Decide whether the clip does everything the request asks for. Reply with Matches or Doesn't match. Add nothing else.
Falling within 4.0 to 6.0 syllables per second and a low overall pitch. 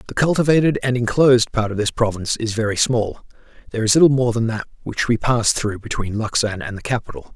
Doesn't match